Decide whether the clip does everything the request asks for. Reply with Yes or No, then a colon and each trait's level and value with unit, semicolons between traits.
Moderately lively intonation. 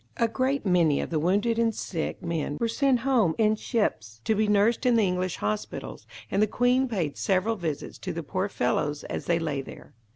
No: wide, 5.9 semitones